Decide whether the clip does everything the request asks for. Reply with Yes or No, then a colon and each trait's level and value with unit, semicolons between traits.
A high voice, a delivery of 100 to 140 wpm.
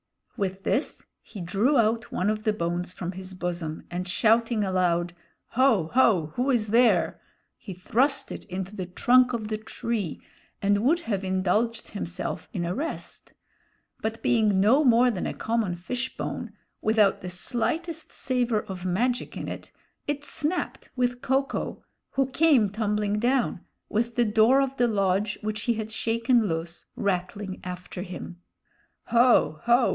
No: high, 215 Hz; average, 160 wpm